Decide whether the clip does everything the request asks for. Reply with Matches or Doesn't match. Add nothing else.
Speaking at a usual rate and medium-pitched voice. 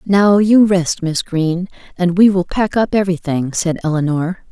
Matches